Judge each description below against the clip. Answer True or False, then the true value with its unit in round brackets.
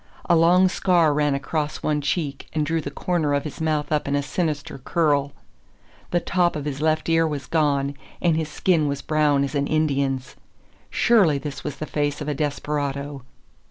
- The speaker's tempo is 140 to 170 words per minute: False (190 wpm)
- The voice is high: False (150 Hz)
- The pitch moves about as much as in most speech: False (2.1 semitones)